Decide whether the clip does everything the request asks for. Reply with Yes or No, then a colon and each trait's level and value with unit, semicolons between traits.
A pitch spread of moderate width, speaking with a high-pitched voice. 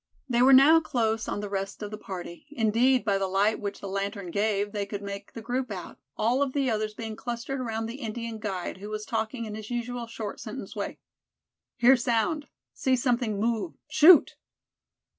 Yes: average, 3.3 semitones; high, 225 Hz